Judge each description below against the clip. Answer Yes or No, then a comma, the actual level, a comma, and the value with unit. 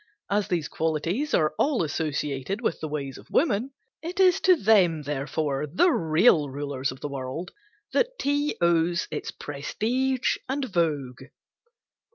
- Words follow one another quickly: No, average, 145 wpm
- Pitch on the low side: No, medium, 165 Hz